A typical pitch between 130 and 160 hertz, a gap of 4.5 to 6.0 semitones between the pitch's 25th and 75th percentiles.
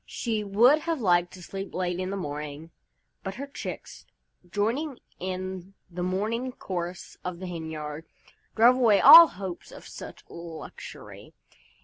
No: medium, 185 Hz; average, 4.8 semitones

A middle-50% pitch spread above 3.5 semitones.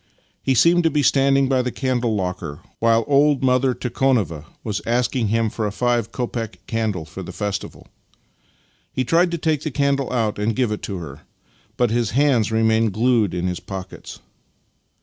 Yes: average, 4.2 semitones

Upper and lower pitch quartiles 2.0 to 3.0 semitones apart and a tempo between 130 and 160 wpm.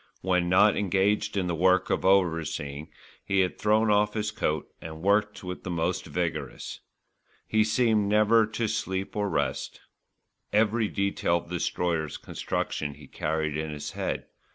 No: average, 4.3 semitones; average, 155 wpm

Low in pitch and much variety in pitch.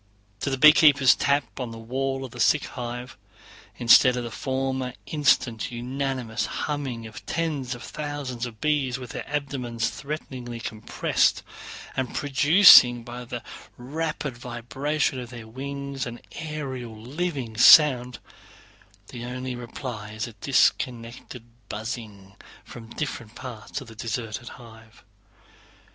No: low, 125 Hz; average, 2.8 semitones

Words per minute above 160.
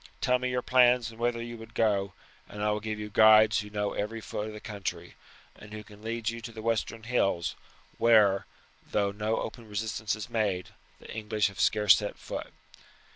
Yes: average, 200 wpm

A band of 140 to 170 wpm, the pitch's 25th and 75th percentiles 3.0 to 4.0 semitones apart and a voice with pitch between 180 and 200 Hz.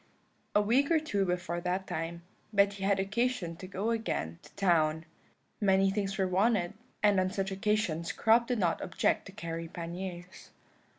Yes: average, 165 wpm; average, 3.3 semitones; high, 190 Hz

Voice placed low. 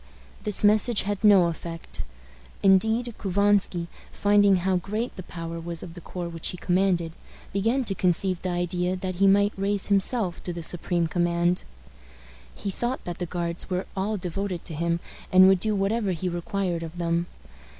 No: medium, 185 Hz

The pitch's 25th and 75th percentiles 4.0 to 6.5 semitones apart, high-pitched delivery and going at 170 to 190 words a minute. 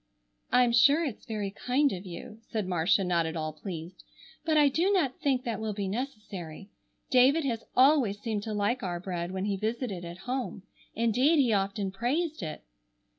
Yes: average, 5.3 semitones; high, 215 Hz; average, 180 wpm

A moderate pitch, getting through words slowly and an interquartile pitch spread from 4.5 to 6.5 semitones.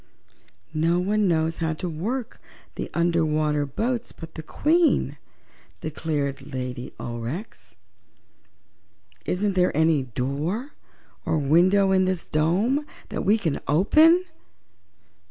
Yes: medium, 165 Hz; slow, 115 wpm; average, 5.1 semitones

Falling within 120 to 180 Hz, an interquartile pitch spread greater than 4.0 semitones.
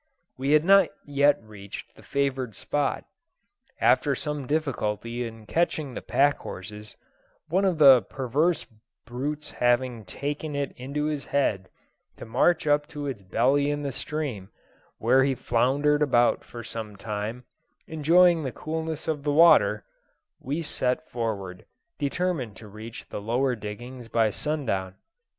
Yes: low, 135 Hz; average, 4.6 semitones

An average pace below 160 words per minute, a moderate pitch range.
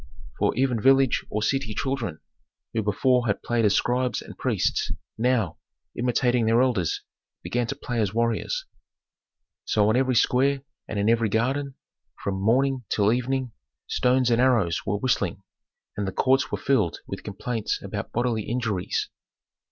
Yes: average, 150 wpm; average, 3.3 semitones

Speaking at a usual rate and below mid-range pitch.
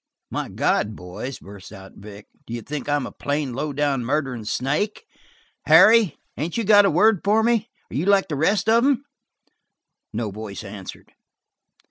No: average, 165 wpm; medium, 145 Hz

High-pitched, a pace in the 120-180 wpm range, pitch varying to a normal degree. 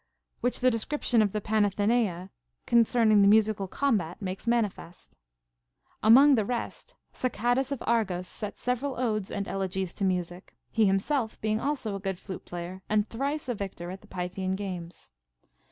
Yes: high, 210 Hz; average, 155 wpm; average, 3.9 semitones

